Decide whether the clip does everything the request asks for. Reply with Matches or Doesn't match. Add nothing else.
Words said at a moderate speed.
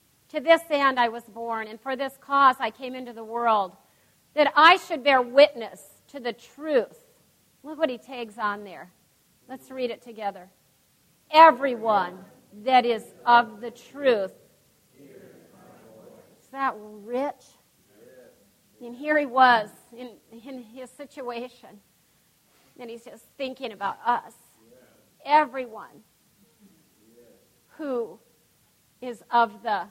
Doesn't match